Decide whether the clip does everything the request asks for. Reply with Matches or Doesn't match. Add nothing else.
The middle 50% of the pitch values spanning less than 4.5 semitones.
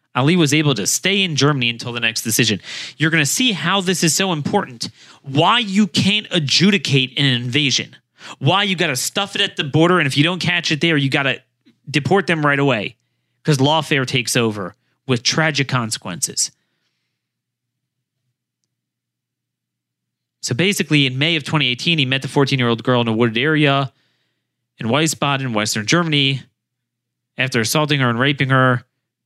Doesn't match